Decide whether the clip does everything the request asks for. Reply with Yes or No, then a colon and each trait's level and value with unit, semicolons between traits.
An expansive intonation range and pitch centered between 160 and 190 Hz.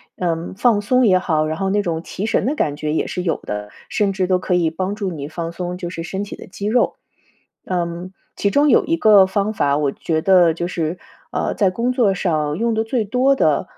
No: average, 4.0 semitones; medium, 185 Hz